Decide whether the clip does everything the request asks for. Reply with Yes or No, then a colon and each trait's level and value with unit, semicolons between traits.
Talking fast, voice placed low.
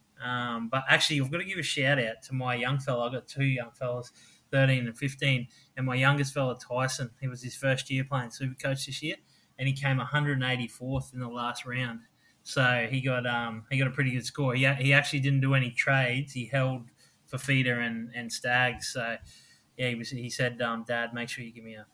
Yes: fast, 230 wpm; low, 130 Hz